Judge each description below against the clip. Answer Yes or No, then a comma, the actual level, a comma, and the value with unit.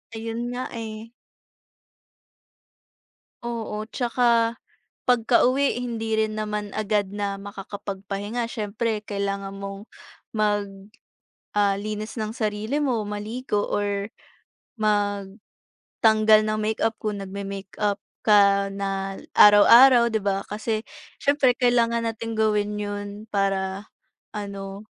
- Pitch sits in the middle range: No, high, 210 Hz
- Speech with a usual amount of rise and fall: No, narrow, 2.1 semitones